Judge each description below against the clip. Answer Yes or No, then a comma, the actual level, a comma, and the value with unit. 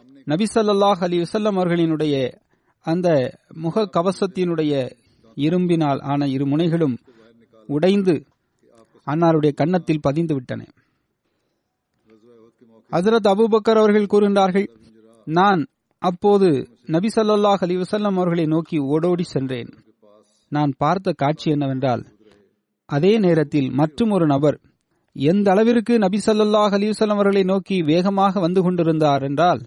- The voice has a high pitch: No, medium, 165 Hz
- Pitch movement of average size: No, wide, 6.0 semitones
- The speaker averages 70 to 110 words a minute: Yes, average, 100 wpm